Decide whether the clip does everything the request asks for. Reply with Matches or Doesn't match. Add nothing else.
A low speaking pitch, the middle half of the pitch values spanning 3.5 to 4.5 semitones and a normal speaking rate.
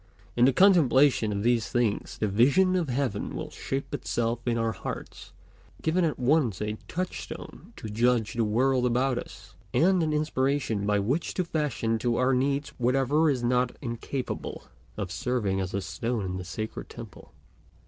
Matches